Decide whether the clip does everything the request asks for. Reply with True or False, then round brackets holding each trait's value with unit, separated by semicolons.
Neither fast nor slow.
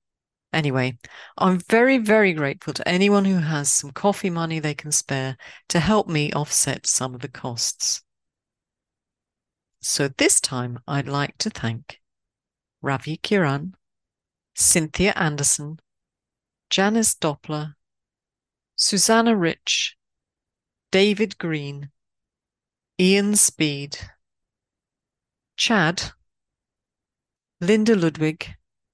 False (95 wpm)